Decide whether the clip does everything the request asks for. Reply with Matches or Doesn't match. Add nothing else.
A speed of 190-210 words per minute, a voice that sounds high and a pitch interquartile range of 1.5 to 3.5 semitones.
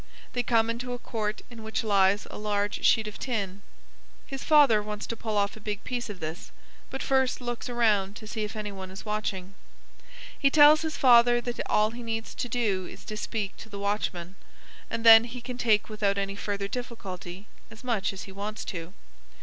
Matches